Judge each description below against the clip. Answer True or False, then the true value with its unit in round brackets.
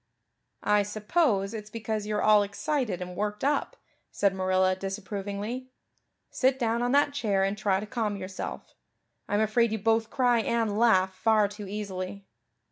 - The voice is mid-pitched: False (210 Hz)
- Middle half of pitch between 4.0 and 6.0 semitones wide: False (2.6 semitones)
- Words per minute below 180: True (155 wpm)